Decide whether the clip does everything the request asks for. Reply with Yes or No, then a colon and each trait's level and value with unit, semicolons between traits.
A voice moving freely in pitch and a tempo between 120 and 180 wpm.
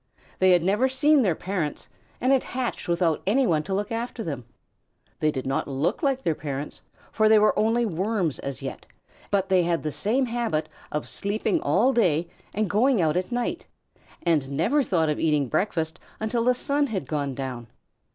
No: wide, 7.2 semitones; average, 190 wpm